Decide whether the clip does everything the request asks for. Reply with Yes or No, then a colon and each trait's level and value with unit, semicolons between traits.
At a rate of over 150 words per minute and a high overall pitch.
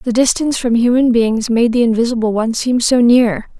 Yes: average, 200 wpm; high, 235 Hz